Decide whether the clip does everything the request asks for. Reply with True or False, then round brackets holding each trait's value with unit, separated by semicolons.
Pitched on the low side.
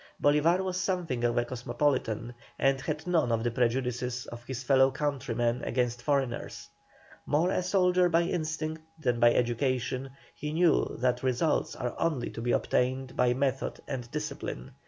True (130 Hz)